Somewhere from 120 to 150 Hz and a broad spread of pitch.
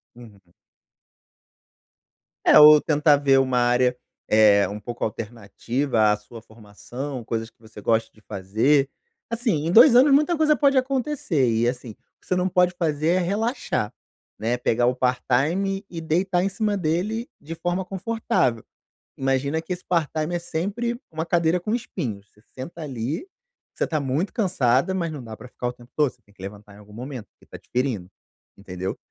Yes: medium, 140 Hz; wide, 7.7 semitones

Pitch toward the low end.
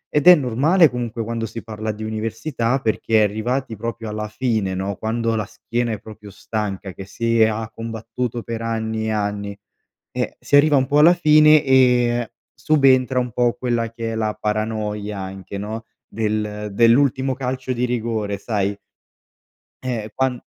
Yes: low, 115 Hz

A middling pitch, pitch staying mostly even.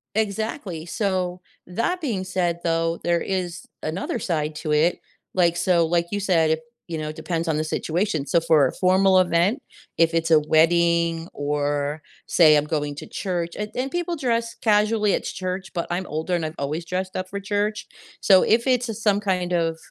No: medium, 175 Hz; average, 3.6 semitones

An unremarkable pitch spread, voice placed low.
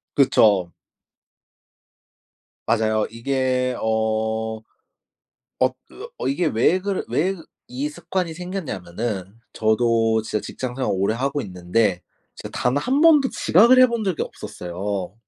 No: wide, 7.7 semitones; low, 120 Hz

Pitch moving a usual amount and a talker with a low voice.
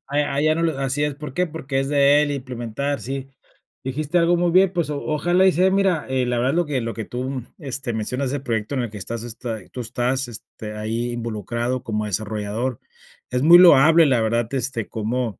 Yes: average, 4.2 semitones; low, 130 Hz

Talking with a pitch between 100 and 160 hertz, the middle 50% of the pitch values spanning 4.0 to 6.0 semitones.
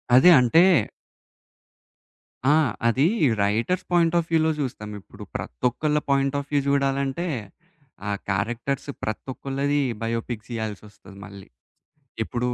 Yes: low, 135 Hz; average, 4.6 semitones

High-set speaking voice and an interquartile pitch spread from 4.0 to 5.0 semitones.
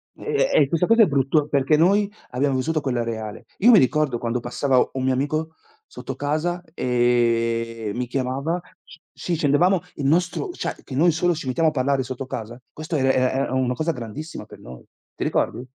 No: low, 135 Hz; average, 4.5 semitones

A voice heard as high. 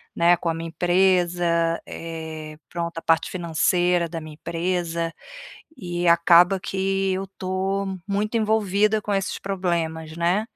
No: medium, 175 Hz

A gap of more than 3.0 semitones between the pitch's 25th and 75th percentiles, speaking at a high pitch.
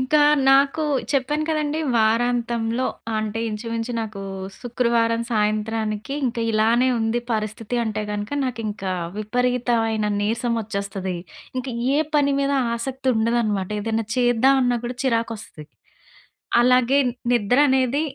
No: narrow, 2.6 semitones; high, 230 Hz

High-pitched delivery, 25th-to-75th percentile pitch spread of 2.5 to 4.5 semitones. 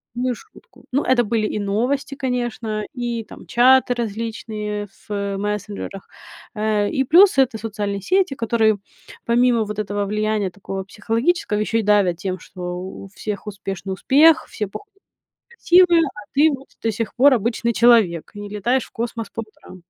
Yes: high, 220 Hz; average, 3.4 semitones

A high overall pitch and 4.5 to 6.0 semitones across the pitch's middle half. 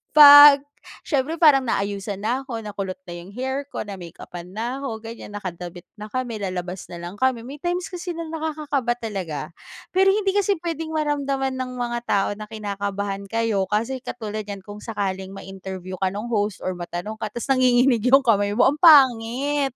Yes: high, 230 Hz; wide, 5.6 semitones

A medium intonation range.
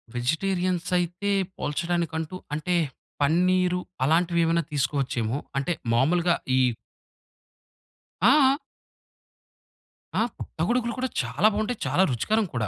Yes: average, 4.1 semitones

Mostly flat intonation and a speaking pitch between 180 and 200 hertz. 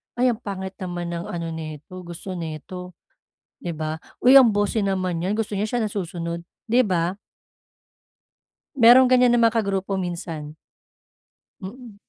No: average, 4.3 semitones; high, 190 Hz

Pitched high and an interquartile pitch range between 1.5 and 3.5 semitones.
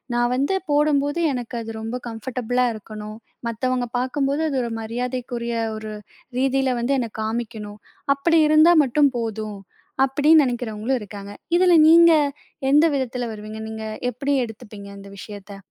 No: high, 245 Hz; average, 3.9 semitones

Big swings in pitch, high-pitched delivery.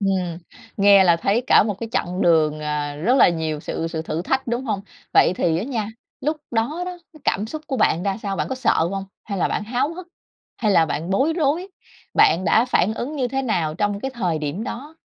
Yes: wide, 7.1 semitones; high, 205 Hz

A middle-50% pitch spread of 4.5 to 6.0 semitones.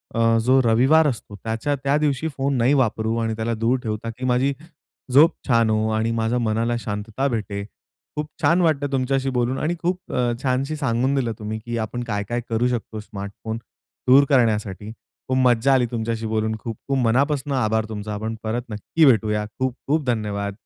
No: average, 3.4 semitones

